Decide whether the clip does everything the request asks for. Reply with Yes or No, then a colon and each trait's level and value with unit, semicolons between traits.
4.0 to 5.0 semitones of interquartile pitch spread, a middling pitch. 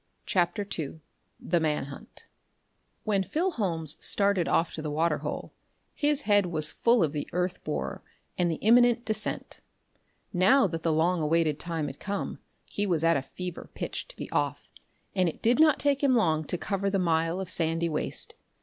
Yes: average, 4.3 semitones; medium, 175 Hz